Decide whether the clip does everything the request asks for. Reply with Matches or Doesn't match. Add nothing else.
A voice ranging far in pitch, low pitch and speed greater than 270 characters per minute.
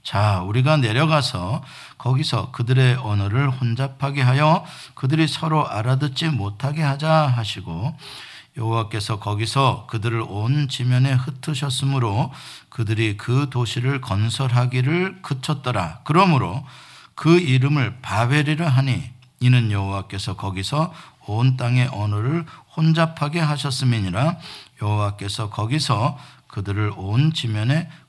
Doesn't match